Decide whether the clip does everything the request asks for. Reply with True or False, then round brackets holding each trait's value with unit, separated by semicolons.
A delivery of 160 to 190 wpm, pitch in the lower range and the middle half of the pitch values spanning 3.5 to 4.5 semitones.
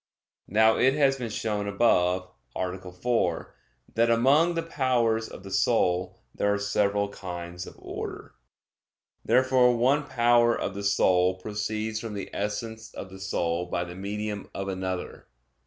False (150 wpm; 105 Hz; 4.0 semitones)